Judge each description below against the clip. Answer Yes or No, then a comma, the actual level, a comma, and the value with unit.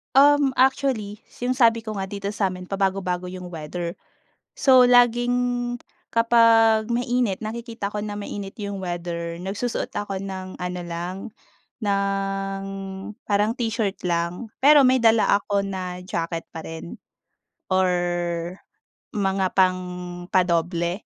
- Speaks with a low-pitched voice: No, high, 200 Hz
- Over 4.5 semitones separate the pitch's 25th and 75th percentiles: No, average, 4.0 semitones